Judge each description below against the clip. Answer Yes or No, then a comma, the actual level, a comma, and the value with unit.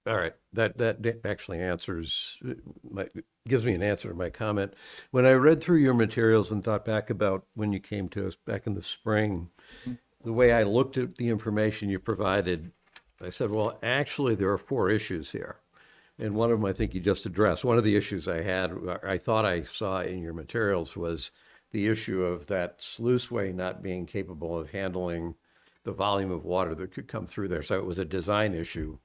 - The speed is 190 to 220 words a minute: Yes, fast, 205 wpm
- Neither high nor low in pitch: No, low, 100 Hz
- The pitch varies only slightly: No, average, 3.6 semitones